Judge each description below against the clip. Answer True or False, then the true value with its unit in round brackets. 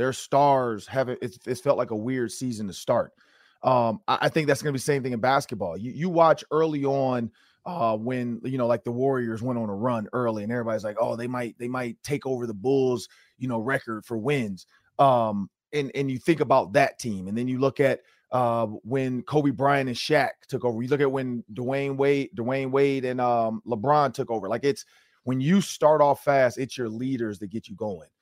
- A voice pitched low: True (125 Hz)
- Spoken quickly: True (225 wpm)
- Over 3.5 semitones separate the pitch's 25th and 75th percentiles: False (2.9 semitones)